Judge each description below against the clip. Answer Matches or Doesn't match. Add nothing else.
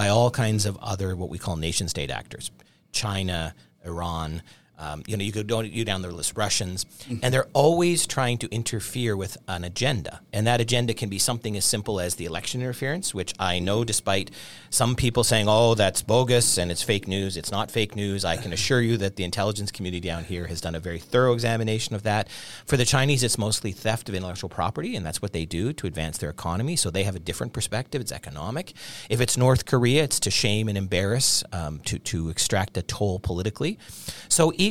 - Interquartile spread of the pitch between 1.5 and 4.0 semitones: Doesn't match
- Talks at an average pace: Doesn't match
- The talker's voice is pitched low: Matches